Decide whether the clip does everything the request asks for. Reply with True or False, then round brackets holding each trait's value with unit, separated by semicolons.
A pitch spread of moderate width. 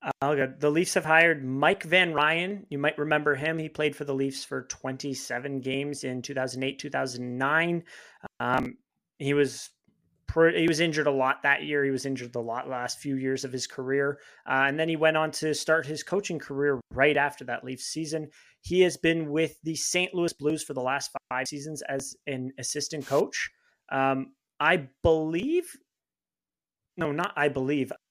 True (3.1 semitones)